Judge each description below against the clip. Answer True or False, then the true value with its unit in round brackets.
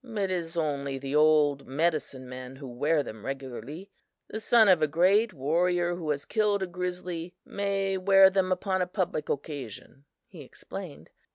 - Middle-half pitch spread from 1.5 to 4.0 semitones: False (5.1 semitones)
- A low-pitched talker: False (170 Hz)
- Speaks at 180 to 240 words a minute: False (165 wpm)